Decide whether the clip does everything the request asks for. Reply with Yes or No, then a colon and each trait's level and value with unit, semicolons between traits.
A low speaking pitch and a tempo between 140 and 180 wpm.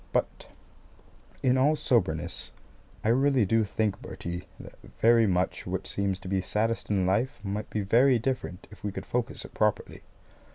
Yes: low, 105 Hz; average, 165 wpm